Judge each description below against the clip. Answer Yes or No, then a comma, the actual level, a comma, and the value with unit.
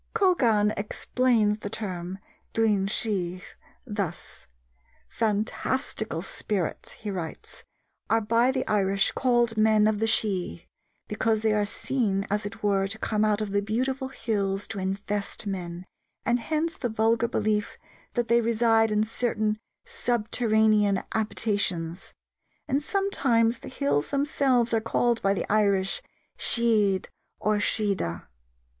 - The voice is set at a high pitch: Yes, high, 215 Hz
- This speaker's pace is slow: Yes, slow, 130 wpm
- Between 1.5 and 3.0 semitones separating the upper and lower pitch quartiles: Yes, narrow, 2.6 semitones